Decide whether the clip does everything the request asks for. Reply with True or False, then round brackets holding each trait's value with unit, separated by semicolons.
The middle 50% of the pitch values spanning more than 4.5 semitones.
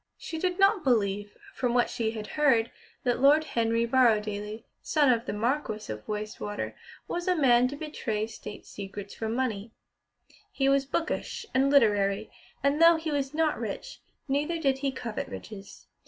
True (5.1 semitones)